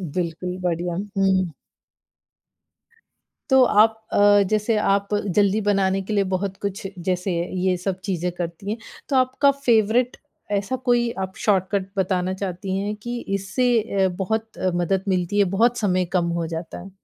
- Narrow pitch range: No, average, 3.0 semitones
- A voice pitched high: Yes, high, 195 Hz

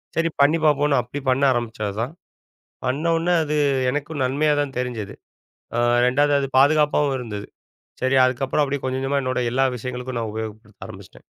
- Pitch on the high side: No, low, 135 Hz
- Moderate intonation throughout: Yes, average, 3.1 semitones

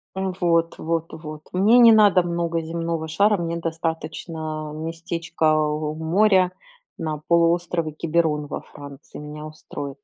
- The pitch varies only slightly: Yes, narrow, 1.8 semitones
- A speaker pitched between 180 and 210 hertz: No, medium, 165 Hz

